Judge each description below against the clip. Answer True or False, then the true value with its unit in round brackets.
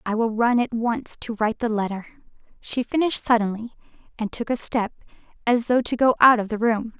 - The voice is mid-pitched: False (230 Hz)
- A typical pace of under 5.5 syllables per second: False (5.6 syllables/s)